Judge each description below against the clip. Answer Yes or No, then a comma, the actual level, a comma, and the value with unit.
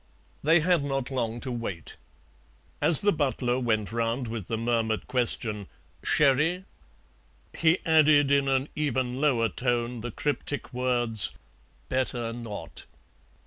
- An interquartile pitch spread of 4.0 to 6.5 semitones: No, average, 3.6 semitones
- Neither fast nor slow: No, slow, 125 wpm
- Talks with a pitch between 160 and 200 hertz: No, low, 125 Hz